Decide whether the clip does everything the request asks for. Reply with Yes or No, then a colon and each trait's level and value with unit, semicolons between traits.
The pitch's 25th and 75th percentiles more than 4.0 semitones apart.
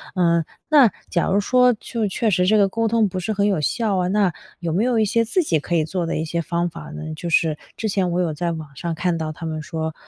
Yes: average, 4.6 semitones